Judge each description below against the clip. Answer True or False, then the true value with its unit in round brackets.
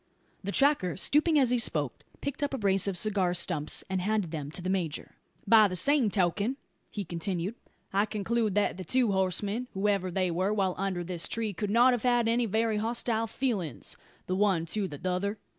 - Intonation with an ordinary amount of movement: True (3.9 semitones)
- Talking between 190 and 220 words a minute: True (195 wpm)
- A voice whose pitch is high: True (200 Hz)